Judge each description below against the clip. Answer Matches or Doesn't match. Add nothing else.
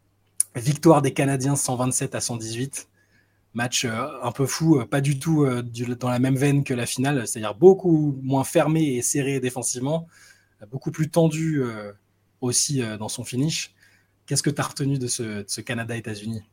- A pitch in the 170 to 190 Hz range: Doesn't match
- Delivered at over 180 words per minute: Doesn't match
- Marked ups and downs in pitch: Doesn't match